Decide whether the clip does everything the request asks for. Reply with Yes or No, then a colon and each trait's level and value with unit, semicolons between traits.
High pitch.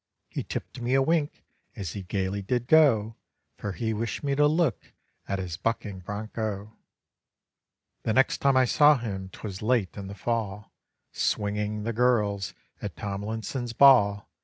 No: low, 110 Hz